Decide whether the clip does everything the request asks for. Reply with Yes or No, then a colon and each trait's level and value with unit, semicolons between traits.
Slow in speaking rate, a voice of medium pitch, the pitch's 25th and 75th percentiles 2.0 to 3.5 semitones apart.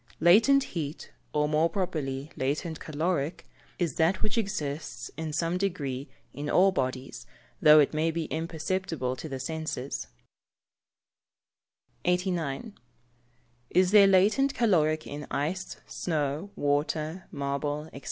No: slow, 125 wpm; medium, 160 Hz; average, 4.0 semitones